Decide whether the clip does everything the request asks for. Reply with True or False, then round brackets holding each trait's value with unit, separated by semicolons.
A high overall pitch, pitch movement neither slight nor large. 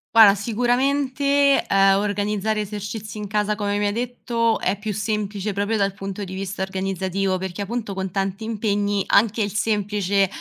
False (205 Hz; 1.9 semitones)